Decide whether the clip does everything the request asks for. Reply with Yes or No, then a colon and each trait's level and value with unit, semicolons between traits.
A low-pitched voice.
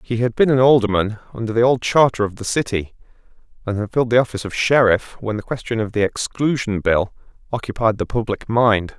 Yes: low, 115 Hz